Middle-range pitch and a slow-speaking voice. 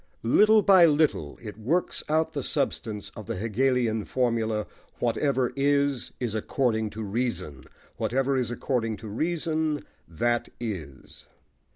No: low, 120 Hz; slow, 130 wpm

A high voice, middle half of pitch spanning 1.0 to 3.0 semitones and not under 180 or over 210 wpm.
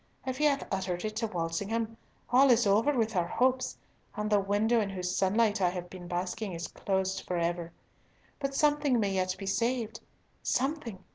No: high, 210 Hz; average, 4.6 semitones; average, 185 wpm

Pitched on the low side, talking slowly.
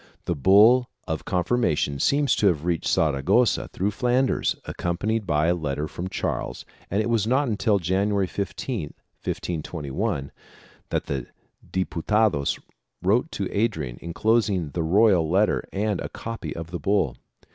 No: very low, 95 Hz; average, 145 wpm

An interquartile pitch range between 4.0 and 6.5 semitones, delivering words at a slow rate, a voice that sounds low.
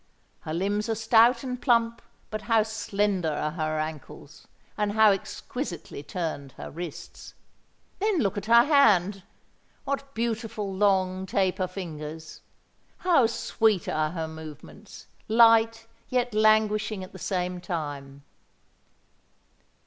No: average, 4.9 semitones; slow, 120 wpm; high, 205 Hz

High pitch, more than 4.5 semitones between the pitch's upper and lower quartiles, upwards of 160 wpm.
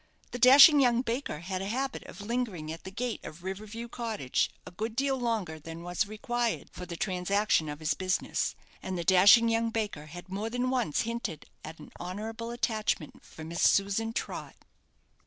Yes: high, 210 Hz; average, 4.9 semitones; average, 185 wpm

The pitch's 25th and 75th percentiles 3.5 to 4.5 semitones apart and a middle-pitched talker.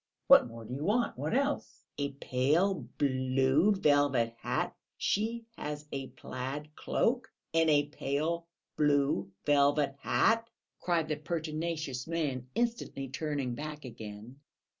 Yes: average, 3.9 semitones; medium, 145 Hz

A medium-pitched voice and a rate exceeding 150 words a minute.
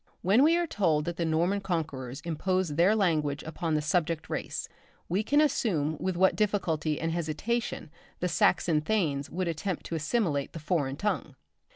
Yes: medium, 170 Hz; average, 170 wpm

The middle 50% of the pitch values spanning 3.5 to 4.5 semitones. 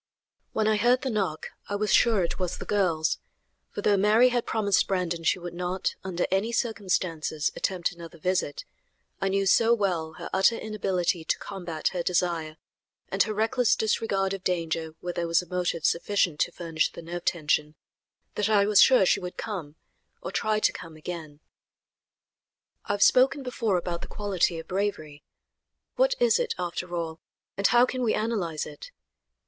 Yes: average, 4.0 semitones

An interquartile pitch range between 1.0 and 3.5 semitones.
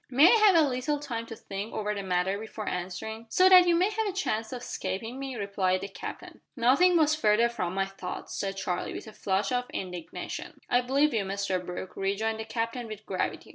No: average, 5.1 semitones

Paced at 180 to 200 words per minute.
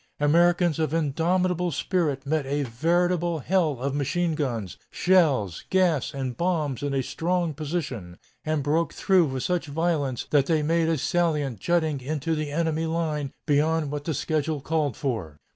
No: average, 160 wpm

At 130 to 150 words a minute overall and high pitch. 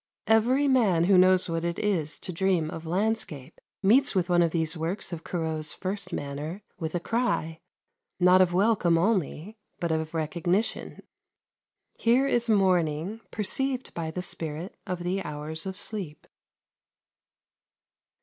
No: average, 140 wpm; medium, 180 Hz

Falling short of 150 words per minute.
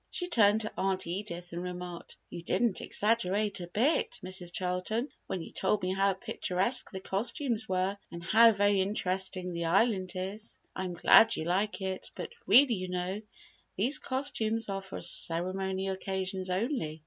No: average, 165 wpm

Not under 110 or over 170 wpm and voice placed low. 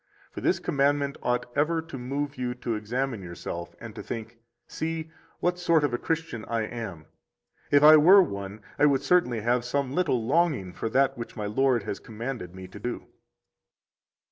No: average, 185 wpm; low, 125 Hz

